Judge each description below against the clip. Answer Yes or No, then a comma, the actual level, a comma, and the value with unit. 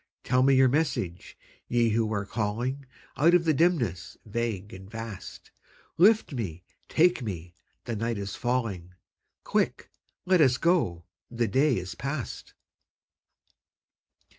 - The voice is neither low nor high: No, low, 120 Hz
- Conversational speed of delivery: No, slow, 130 wpm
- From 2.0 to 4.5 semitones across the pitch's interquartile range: No, wide, 5.4 semitones